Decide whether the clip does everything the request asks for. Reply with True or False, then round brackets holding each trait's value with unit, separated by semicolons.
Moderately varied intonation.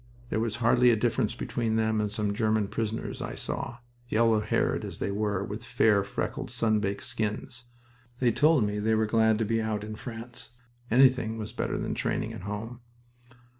False (1.7 semitones)